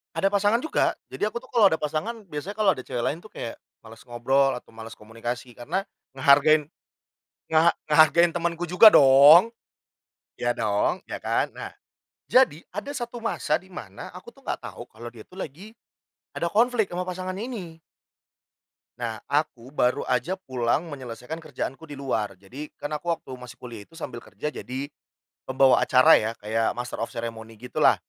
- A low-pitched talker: No, medium, 145 Hz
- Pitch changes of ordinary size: No, wide, 6.8 semitones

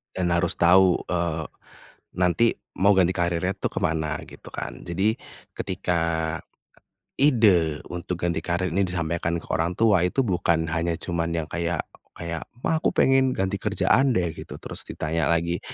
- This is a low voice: Yes, very low, 85 Hz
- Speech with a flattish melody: Yes, narrow, 2.3 semitones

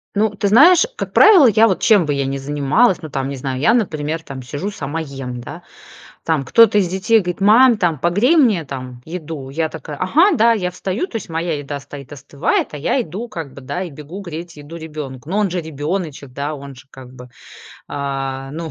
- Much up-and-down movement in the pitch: Yes, wide, 6.1 semitones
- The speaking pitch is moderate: Yes, medium, 160 Hz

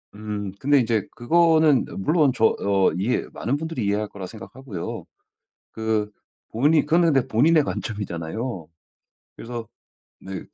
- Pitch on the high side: No, low, 115 Hz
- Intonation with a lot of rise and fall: Yes, wide, 5.9 semitones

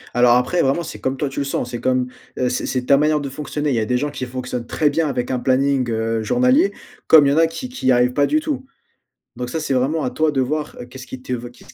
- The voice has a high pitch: No, low, 135 Hz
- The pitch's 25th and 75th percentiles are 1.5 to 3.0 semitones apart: No, average, 3.5 semitones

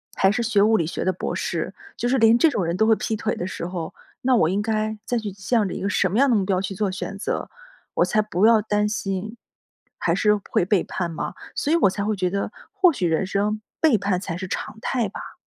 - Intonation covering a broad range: No, average, 2.9 semitones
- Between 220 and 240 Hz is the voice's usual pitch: No, high, 210 Hz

